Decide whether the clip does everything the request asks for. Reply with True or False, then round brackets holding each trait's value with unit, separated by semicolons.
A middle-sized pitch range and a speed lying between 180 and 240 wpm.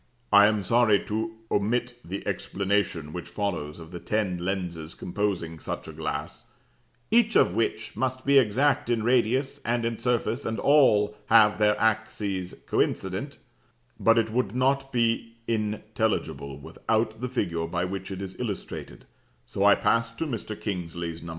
False (3.8 semitones; 155 wpm)